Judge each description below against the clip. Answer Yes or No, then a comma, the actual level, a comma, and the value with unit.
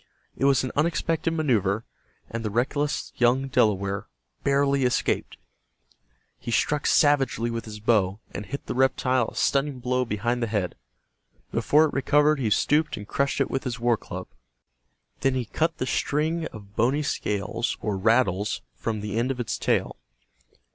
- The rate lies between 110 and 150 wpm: No, average, 160 wpm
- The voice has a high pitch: No, low, 125 Hz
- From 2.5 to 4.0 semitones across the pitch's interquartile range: No, average, 4.7 semitones